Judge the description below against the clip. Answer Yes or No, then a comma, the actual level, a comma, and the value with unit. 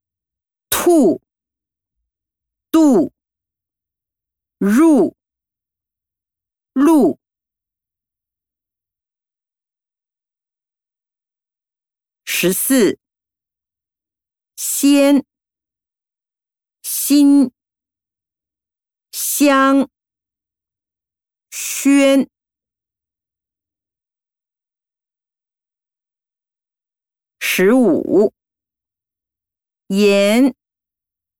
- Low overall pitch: Yes, low, 105 Hz